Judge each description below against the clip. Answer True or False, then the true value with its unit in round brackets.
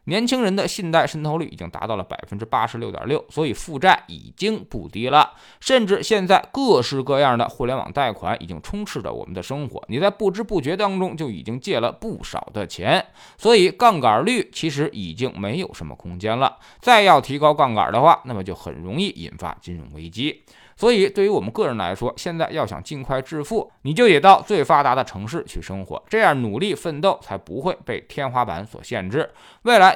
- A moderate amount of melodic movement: False (8.8 semitones)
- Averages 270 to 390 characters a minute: True (315 characters per minute)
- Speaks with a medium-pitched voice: True (155 Hz)